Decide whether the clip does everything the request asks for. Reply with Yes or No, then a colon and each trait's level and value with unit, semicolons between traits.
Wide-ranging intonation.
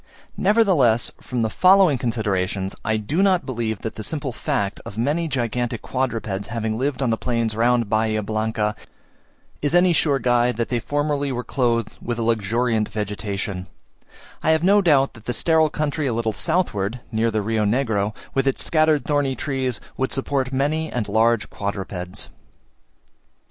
No: average, 4.5 semitones